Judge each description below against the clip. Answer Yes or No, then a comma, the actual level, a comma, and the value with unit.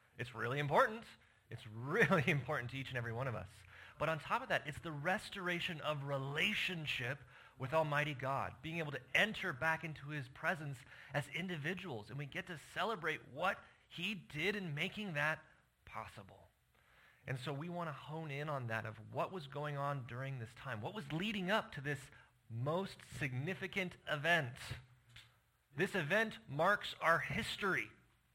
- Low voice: No, medium, 145 Hz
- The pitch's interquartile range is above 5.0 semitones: Yes, wide, 5.5 semitones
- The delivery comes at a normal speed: Yes, average, 165 wpm